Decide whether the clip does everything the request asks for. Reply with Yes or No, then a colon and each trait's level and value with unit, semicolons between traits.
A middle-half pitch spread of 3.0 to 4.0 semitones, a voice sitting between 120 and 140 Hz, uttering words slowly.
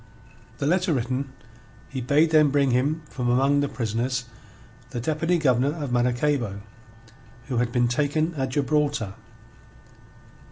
Yes: average, 3.4 semitones; low, 135 Hz; slow, 130 wpm